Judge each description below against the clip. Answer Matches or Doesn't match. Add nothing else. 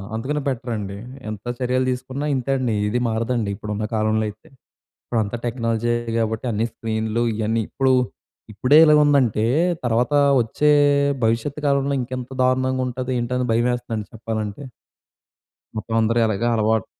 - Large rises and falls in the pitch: Doesn't match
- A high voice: Doesn't match